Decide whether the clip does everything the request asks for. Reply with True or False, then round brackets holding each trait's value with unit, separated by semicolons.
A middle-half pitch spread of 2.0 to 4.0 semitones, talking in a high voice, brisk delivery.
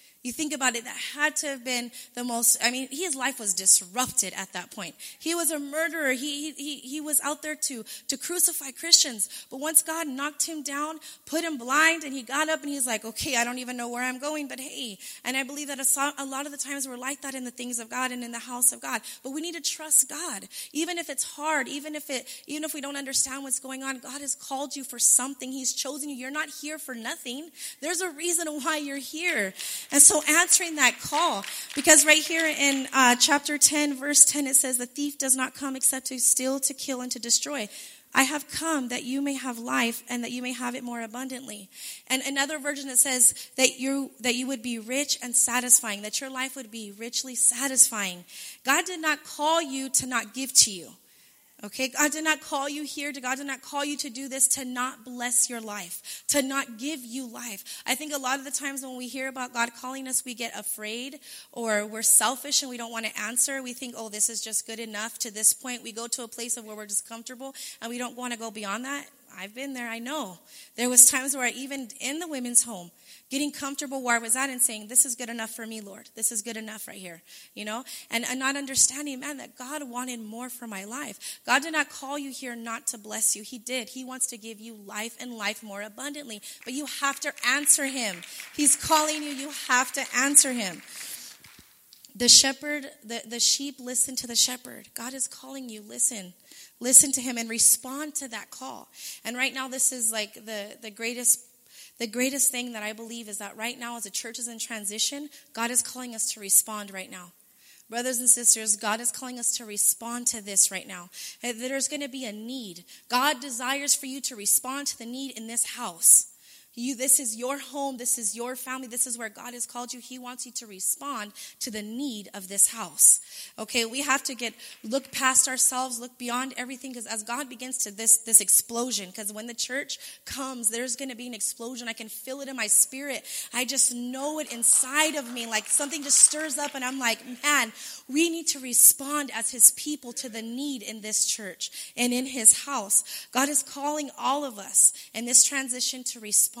True (3.2 semitones; 255 Hz; 230 wpm)